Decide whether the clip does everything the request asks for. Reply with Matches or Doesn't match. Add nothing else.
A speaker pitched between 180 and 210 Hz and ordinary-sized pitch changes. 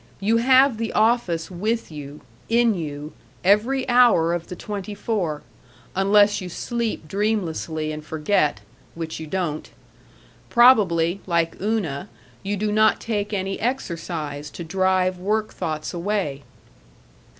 Matches